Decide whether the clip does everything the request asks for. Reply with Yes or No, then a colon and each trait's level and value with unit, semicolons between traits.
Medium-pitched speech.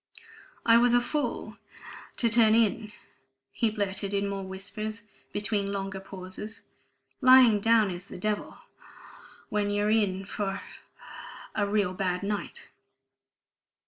No: high, 205 Hz